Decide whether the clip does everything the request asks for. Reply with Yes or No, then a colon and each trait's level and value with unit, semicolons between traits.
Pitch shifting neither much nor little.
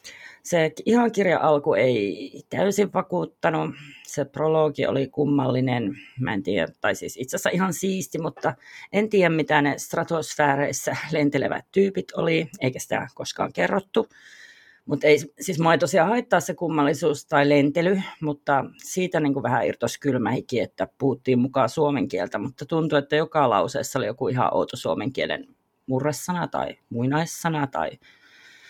Yes: average, 4.3 semitones